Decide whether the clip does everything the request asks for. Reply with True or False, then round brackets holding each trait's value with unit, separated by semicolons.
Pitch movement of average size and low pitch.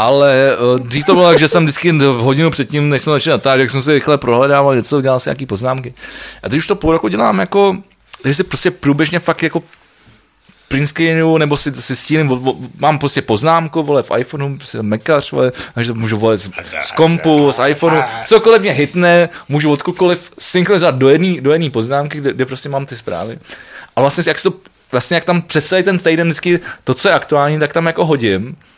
False (3.8 semitones; 145 Hz)